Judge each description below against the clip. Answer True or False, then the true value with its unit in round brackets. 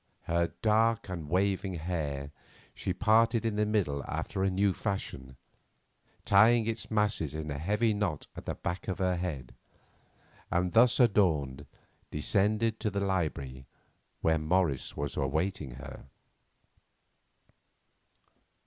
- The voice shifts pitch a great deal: True (5.7 semitones)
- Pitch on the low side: True (95 Hz)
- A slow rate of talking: True (125 wpm)